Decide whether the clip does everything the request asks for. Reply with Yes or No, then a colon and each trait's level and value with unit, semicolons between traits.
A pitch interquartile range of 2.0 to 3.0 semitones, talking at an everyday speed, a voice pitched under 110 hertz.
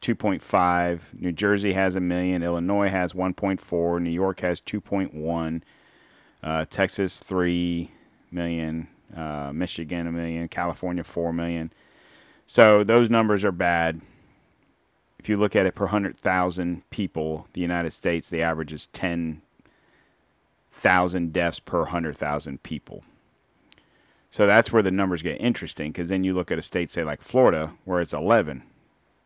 Yes: narrow, 2.4 semitones; average, 145 wpm; very low, 85 Hz